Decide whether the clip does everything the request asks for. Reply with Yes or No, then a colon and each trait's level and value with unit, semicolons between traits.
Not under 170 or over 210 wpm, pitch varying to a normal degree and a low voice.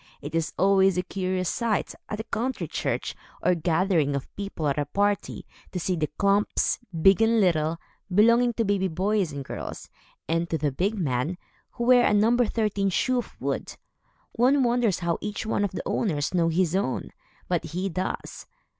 No: average, 180 wpm; average, 4.4 semitones; high, 190 Hz